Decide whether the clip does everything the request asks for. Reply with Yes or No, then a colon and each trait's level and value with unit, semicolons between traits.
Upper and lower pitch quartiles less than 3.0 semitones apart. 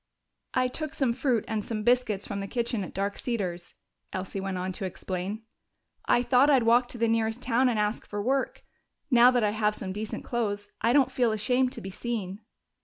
No: average, 3.4 semitones